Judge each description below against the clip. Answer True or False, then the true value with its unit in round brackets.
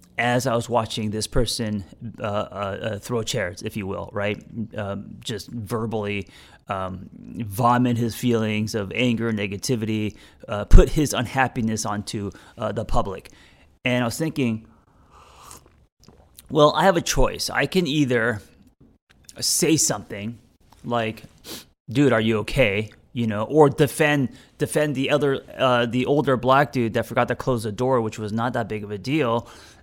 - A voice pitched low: True (120 Hz)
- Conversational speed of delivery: True (155 wpm)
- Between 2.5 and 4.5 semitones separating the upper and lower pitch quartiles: True (3.5 semitones)